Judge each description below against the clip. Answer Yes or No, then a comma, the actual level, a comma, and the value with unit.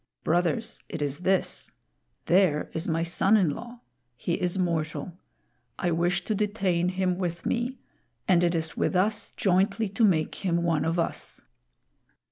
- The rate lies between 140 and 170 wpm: Yes, average, 155 wpm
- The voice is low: No, medium, 180 Hz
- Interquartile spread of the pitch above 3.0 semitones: No, average, 2.7 semitones